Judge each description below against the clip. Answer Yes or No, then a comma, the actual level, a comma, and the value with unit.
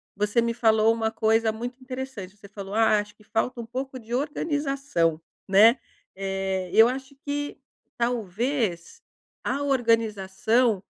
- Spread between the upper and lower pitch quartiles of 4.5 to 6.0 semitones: No, average, 3.9 semitones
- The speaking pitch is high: Yes, high, 225 Hz